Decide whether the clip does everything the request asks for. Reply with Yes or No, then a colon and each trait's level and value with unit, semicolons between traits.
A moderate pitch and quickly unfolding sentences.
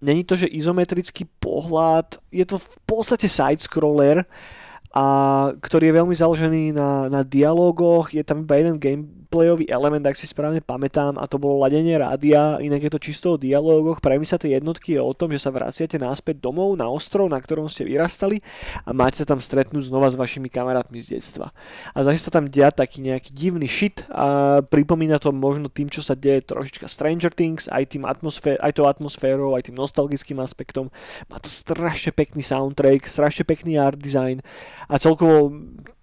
Yes: medium, 145 Hz; fast, 185 wpm